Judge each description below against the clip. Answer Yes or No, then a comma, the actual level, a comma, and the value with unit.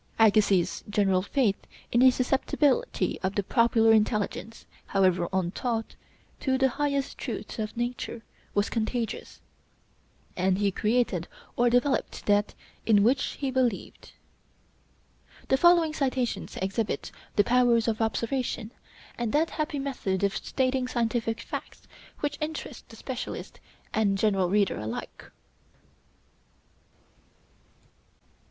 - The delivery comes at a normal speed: No, slow, 115 wpm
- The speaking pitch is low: No, high, 230 Hz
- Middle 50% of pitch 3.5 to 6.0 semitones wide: Yes, average, 4.3 semitones